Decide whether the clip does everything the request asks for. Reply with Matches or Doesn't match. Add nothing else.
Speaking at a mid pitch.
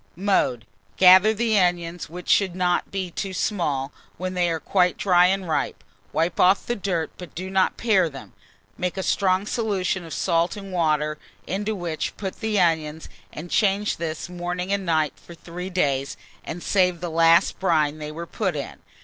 Matches